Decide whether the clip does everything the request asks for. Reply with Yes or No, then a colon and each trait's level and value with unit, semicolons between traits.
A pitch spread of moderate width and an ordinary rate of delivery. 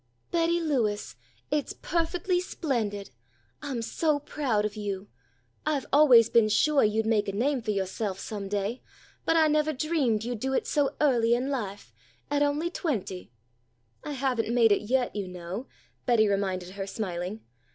No: wide, 6.0 semitones; average, 160 wpm